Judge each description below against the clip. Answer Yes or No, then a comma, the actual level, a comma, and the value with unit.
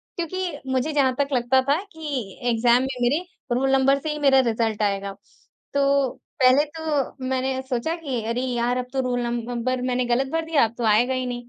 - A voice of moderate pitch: No, very high, 255 Hz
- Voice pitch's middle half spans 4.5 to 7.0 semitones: No, average, 2.7 semitones